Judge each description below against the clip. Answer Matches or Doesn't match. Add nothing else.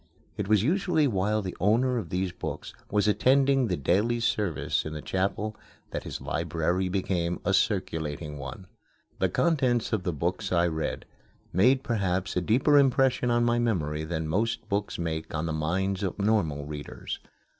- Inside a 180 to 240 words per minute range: Doesn't match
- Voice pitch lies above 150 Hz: Doesn't match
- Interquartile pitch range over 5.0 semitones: Matches